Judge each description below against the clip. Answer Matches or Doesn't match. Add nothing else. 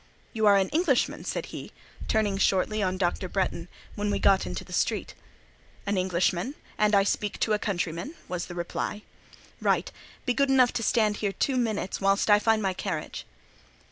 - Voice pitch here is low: Doesn't match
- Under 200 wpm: Matches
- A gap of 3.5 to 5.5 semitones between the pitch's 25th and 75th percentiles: Doesn't match